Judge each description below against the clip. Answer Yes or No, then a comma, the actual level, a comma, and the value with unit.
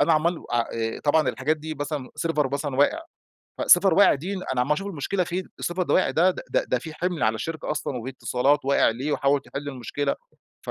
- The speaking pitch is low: No, medium, 145 Hz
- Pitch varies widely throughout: No, average, 3.7 semitones